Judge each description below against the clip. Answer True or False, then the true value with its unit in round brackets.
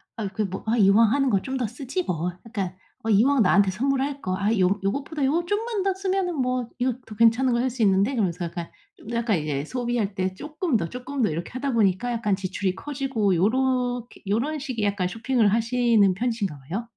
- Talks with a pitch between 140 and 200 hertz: False (230 Hz)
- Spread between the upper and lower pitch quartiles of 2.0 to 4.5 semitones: False (5.1 semitones)